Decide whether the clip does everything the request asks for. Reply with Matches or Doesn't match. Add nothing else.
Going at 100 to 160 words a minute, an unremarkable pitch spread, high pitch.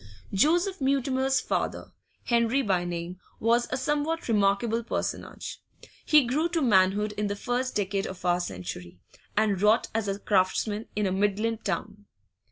Matches